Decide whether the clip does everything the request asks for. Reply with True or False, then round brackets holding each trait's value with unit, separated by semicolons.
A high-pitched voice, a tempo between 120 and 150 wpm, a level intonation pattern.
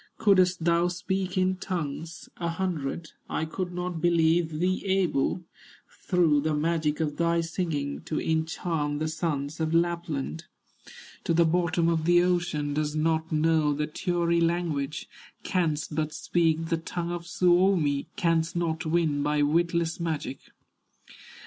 False (165 Hz; 140 wpm; 2.2 semitones)